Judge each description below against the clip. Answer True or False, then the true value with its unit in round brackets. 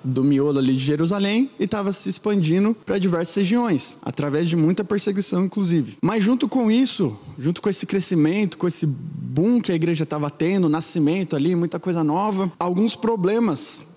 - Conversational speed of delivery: True (170 wpm)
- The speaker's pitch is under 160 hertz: False (175 Hz)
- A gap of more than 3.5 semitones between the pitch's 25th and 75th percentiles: True (4.4 semitones)